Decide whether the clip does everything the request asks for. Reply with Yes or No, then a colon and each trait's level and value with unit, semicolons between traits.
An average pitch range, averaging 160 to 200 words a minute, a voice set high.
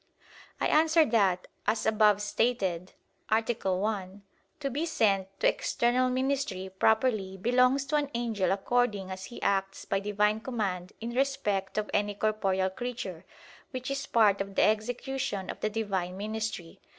No: average, 4.1 semitones; average, 150 wpm; high, 215 Hz